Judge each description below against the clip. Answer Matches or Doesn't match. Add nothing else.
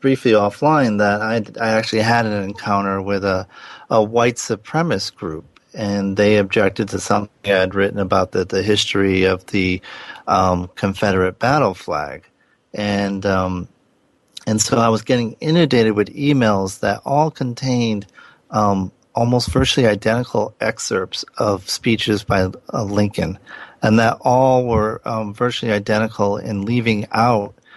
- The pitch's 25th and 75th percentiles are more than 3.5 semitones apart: Doesn't match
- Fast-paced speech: Doesn't match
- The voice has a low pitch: Matches